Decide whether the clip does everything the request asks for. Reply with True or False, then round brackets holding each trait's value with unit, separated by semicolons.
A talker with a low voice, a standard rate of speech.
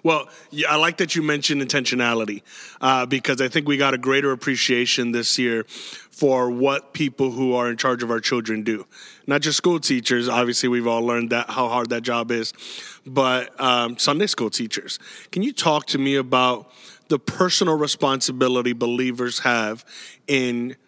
True (130 Hz; 170 wpm)